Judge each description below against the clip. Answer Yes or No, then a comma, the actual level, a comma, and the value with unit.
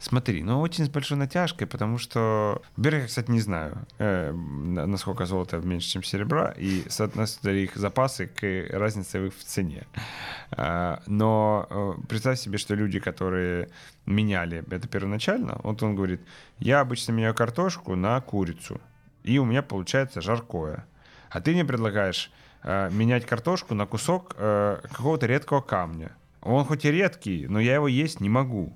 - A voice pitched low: Yes, low, 110 Hz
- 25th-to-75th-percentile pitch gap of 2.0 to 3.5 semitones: No, wide, 5.4 semitones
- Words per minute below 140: No, fast, 155 wpm